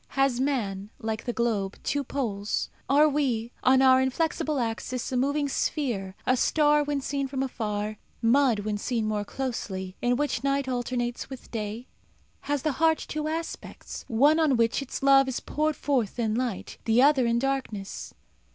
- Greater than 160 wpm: Yes, average, 170 wpm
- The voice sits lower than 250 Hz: No, very high, 255 Hz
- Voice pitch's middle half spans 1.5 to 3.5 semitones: No, average, 3.9 semitones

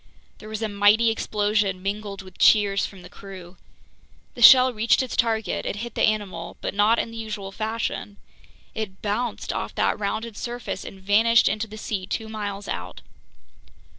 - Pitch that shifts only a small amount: Yes, narrow, 2.0 semitones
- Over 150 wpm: Yes, average, 165 wpm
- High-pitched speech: Yes, high, 210 Hz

